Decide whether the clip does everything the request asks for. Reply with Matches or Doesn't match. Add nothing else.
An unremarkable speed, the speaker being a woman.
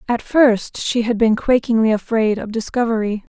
Matches